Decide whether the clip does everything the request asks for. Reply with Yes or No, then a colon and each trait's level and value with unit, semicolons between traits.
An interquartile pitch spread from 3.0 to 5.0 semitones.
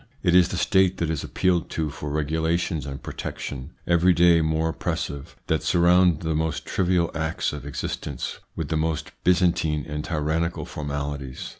No: narrow, 2.6 semitones